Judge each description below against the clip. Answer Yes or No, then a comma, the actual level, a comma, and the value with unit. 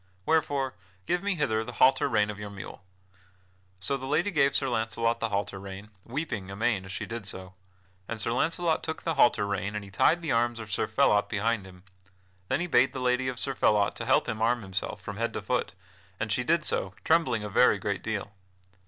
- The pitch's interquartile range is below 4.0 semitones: No, average, 4.9 semitones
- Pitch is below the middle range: Yes, low, 115 Hz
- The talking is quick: Yes, fast, 215 wpm